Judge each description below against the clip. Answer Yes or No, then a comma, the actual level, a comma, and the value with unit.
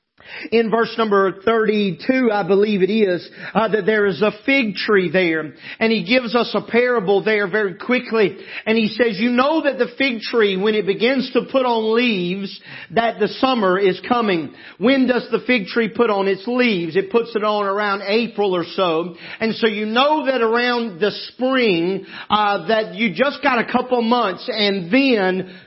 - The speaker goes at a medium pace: Yes, average, 190 wpm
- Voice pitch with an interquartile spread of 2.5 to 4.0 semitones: Yes, average, 3.5 semitones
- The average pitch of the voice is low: No, high, 220 Hz